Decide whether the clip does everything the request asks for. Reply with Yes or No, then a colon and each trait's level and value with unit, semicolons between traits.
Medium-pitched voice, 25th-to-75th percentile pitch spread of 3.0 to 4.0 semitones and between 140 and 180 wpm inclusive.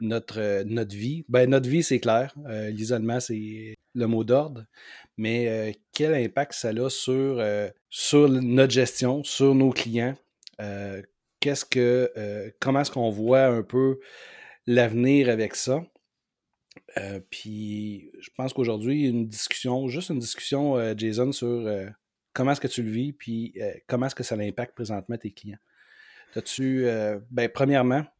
No: low, 120 Hz; average, 3.3 semitones; average, 160 wpm